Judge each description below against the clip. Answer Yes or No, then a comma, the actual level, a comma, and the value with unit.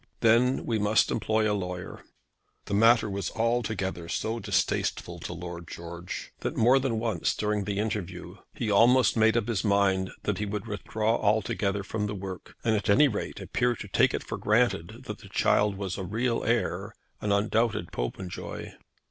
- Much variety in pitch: No, average, 2.8 semitones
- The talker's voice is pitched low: Yes, low, 105 Hz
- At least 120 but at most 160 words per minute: No, average, 175 wpm